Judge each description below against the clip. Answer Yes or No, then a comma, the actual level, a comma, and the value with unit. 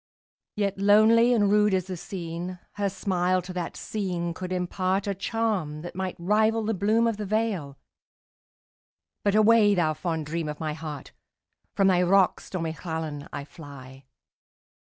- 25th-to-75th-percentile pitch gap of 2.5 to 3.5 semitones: No, average, 3.9 semitones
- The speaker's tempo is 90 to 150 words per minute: Yes, average, 140 wpm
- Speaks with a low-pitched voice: No, medium, 185 Hz